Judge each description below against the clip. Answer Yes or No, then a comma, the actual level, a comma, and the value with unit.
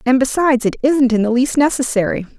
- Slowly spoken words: No, average, 200 wpm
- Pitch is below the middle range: No, very high, 255 Hz